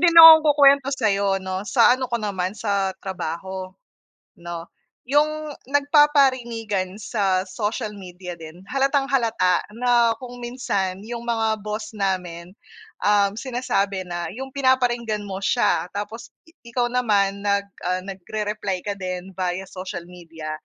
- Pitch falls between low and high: No, high, 205 Hz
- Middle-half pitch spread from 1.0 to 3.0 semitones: No, average, 4.7 semitones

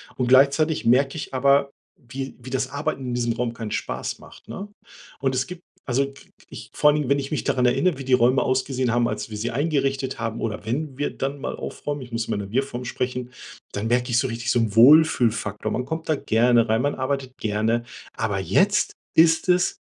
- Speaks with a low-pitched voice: Yes, low, 130 Hz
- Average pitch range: Yes, average, 3.0 semitones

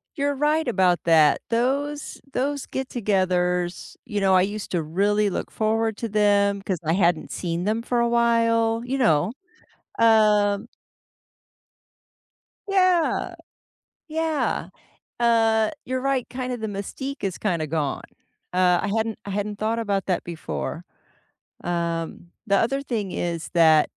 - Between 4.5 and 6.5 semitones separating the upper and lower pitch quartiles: Yes, average, 4.8 semitones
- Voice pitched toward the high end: Yes, high, 210 Hz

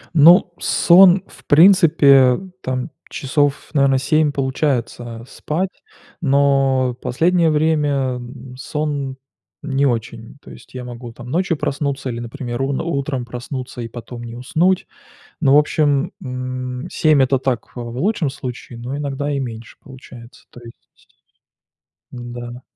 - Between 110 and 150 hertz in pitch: Yes, low, 135 Hz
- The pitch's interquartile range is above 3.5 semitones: No, average, 3.2 semitones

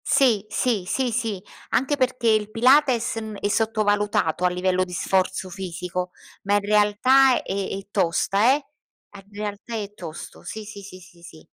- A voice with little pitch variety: No, average, 3.6 semitones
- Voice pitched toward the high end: Yes, high, 205 Hz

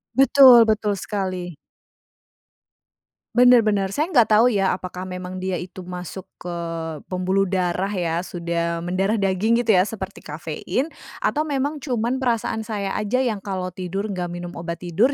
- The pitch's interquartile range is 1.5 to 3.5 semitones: No, average, 3.9 semitones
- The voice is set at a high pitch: Yes, high, 195 Hz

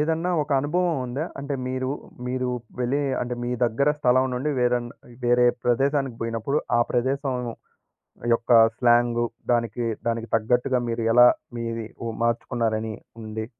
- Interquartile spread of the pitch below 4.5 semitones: Yes, narrow, 2.4 semitones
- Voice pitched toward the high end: No, low, 125 Hz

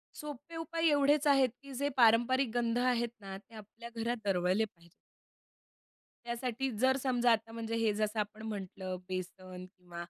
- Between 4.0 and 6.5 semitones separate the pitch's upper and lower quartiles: Yes, average, 4.4 semitones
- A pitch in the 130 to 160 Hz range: No, high, 230 Hz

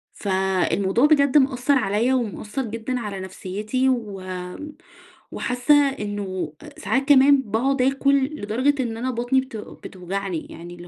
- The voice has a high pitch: Yes, high, 230 Hz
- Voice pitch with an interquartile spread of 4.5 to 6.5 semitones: Yes, average, 5.1 semitones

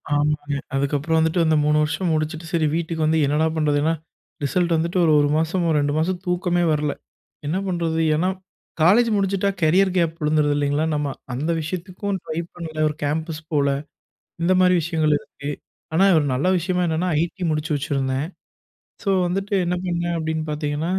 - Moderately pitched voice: Yes, medium, 160 Hz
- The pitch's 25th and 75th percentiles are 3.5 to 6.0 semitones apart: No, average, 2.7 semitones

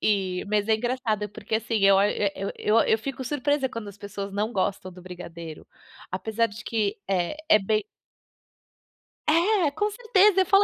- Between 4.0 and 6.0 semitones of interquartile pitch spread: Yes, average, 5.3 semitones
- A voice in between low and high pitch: No, high, 215 Hz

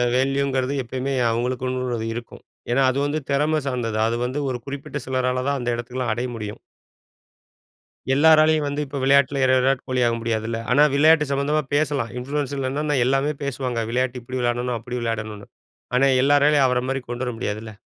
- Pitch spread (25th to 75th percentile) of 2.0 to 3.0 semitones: Yes, narrow, 2.5 semitones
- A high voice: No, low, 130 Hz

